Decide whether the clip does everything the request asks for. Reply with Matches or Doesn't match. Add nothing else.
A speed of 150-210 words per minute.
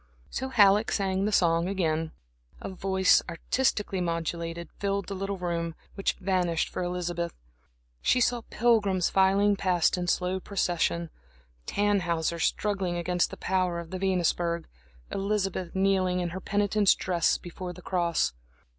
Doesn't match